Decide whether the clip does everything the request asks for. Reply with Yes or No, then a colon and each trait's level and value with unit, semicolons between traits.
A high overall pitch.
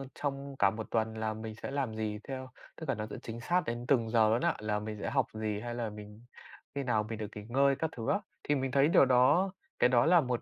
No: low, 120 Hz